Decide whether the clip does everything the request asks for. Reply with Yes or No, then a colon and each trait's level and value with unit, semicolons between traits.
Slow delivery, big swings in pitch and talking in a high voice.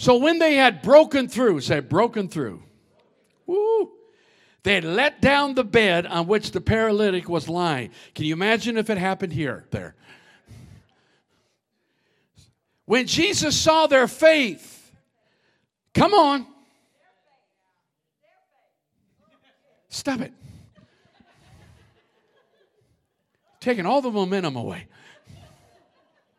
Yes: slow, 100 wpm; wide, 8.3 semitones; high, 225 Hz